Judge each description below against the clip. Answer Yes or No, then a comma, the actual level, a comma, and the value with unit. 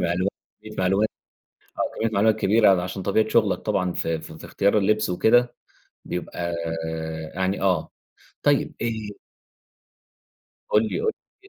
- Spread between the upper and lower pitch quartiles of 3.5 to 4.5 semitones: No, average, 3.1 semitones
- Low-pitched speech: Yes, low, 100 Hz